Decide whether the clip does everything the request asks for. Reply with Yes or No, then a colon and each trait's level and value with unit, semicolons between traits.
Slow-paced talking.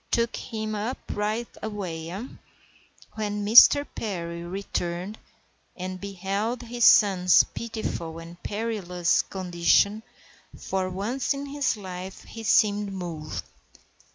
Yes: slow, 110 wpm